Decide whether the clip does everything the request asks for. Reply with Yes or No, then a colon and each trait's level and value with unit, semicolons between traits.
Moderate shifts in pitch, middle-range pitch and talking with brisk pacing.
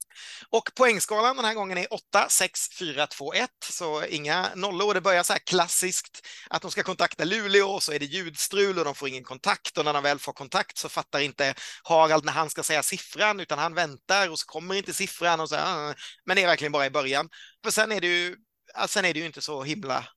Yes: average, 4.5 semitones; medium, 175 Hz; fast, 235 wpm